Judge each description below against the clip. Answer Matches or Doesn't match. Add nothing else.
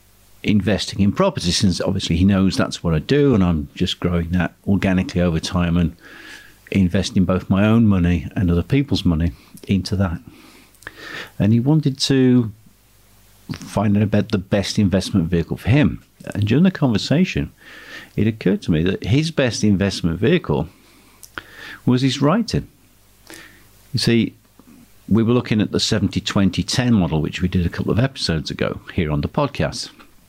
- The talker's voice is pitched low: Matches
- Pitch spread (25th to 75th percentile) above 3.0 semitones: Matches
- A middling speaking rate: Matches